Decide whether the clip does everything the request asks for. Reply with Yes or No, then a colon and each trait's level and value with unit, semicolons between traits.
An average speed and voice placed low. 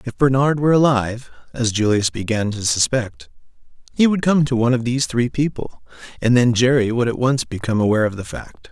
Yes: average, 185 wpm; low, 120 Hz